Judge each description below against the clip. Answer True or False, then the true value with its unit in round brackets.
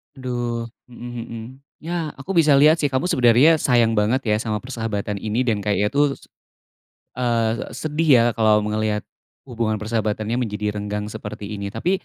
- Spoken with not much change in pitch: False (3.2 semitones)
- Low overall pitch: True (115 Hz)